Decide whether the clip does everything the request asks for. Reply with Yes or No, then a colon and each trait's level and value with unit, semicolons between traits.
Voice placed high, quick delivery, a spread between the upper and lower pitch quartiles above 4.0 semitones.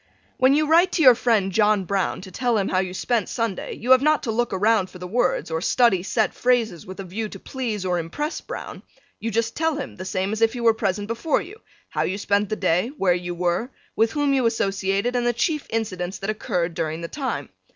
Yes: high, 215 Hz; fast, 235 wpm; average, 4.6 semitones